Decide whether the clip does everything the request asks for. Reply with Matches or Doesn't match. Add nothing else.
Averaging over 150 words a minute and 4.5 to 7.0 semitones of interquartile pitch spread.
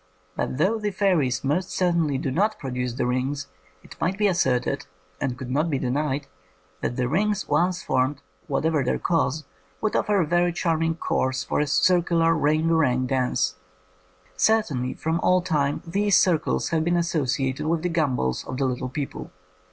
Matches